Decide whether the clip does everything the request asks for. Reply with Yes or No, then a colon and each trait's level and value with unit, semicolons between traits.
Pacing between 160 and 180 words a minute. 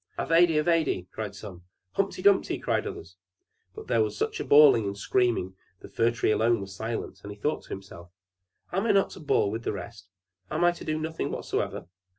No: average, 200 wpm